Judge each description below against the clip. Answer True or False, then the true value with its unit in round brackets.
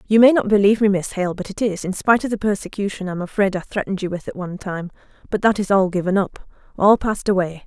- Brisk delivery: True (245 wpm)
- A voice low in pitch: False (195 Hz)